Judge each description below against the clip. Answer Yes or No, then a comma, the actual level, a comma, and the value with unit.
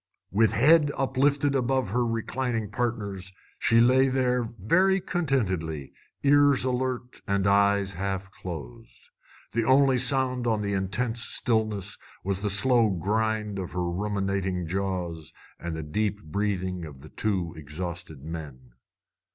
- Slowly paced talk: Yes, slow, 130 wpm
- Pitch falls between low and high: No, low, 105 Hz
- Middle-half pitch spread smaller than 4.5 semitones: No, wide, 5.4 semitones